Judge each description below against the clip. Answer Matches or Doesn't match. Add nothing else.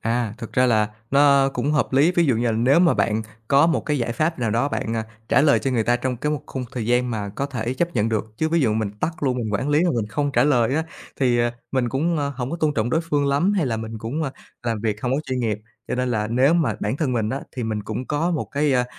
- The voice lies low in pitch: Matches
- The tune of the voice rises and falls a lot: Doesn't match